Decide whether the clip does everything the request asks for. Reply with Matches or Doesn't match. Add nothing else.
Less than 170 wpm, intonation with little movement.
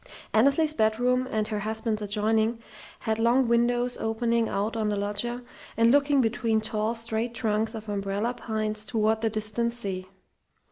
Matches